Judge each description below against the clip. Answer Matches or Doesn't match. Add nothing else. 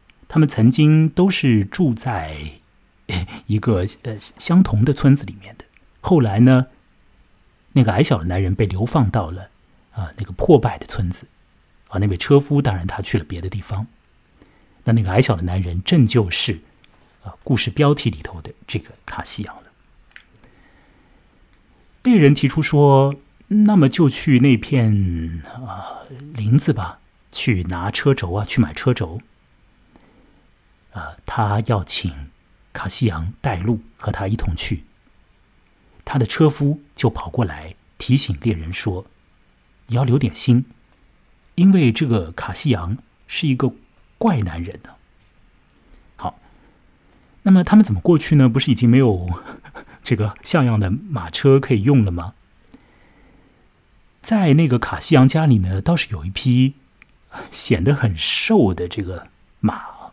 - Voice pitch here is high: Doesn't match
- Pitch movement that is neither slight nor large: Doesn't match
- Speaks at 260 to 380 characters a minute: Doesn't match